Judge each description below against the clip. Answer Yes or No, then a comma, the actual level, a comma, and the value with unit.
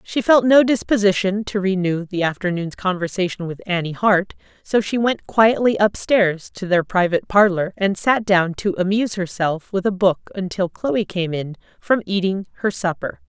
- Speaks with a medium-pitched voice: No, high, 195 Hz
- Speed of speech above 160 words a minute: Yes, average, 170 wpm